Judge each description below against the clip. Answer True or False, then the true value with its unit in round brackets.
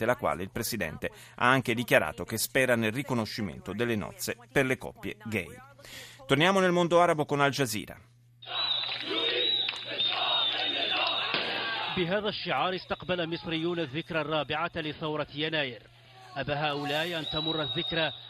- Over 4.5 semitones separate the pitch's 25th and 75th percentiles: True (5.3 semitones)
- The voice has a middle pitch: True (145 Hz)